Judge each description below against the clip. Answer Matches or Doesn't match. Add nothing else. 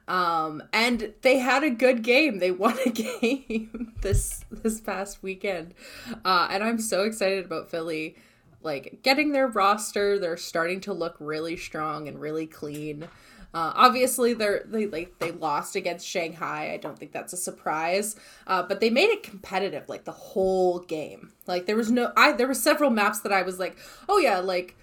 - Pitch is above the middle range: Matches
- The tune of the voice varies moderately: Doesn't match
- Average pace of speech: Matches